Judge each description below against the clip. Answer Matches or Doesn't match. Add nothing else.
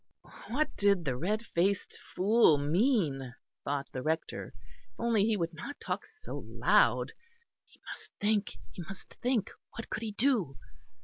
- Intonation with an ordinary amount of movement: Doesn't match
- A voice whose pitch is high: Matches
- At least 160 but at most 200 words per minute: Doesn't match